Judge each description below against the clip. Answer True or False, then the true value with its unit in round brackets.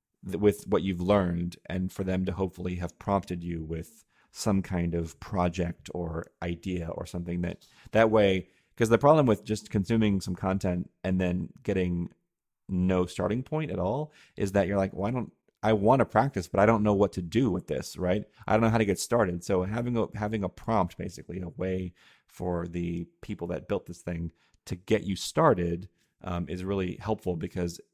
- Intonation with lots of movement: False (3.0 semitones)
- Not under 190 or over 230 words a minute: True (200 wpm)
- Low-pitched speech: True (95 Hz)